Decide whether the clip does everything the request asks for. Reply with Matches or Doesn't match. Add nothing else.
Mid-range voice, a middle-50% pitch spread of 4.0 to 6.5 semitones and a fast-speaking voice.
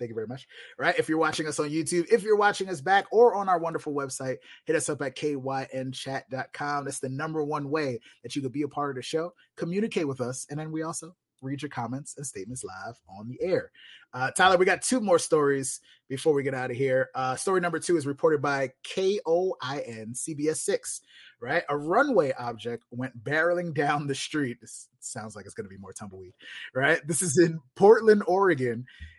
Matches